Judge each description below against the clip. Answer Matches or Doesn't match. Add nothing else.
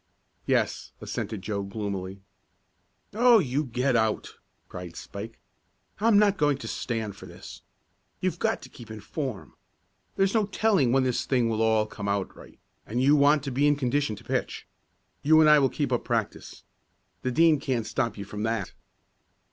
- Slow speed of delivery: Doesn't match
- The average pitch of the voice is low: Matches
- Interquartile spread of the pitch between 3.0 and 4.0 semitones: Doesn't match